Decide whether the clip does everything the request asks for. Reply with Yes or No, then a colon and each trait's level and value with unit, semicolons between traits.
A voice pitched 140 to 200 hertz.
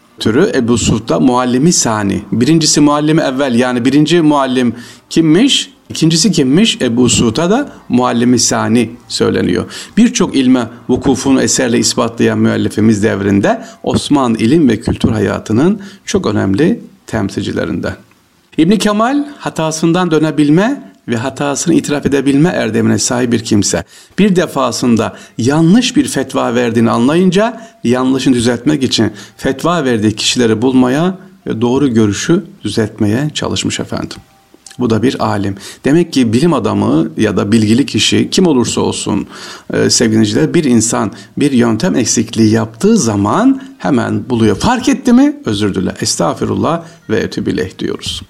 No: low, 130 Hz